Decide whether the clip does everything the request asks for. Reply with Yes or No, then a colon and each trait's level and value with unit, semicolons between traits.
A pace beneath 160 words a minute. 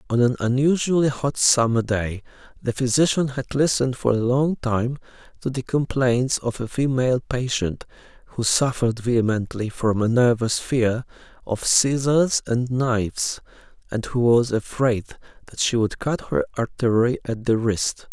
Yes: average, 150 wpm